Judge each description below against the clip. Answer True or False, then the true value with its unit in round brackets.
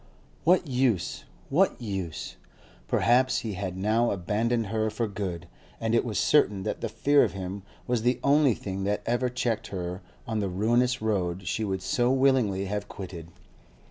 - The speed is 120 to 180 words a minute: True (170 wpm)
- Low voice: True (110 Hz)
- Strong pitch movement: False (4.3 semitones)